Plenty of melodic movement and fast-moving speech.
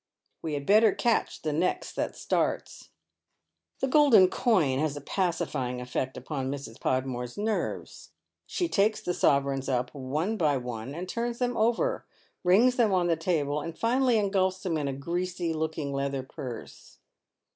No: wide, 7.1 semitones; average, 155 wpm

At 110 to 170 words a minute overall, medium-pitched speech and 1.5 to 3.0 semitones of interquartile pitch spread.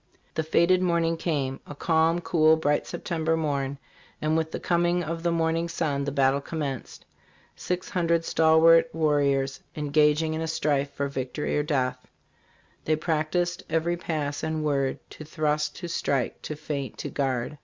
Yes: average, 165 wpm; medium, 155 Hz; narrow, 2.6 semitones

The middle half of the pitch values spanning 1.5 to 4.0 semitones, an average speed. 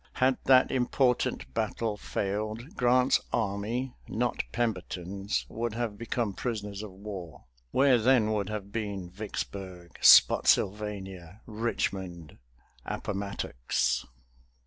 No: average, 3.5 semitones; slow, 100 wpm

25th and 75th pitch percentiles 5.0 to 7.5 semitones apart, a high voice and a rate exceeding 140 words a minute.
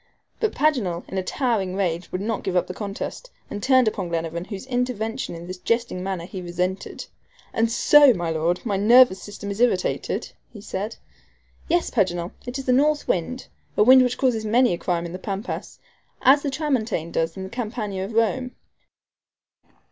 Yes: average, 5.3 semitones; high, 205 Hz; average, 185 wpm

